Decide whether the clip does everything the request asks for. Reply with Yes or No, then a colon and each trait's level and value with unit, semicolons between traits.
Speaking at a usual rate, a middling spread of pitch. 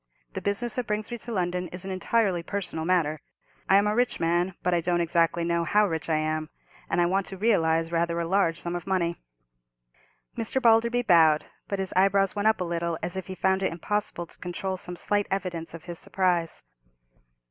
No: fast, 210 wpm; average, 3.0 semitones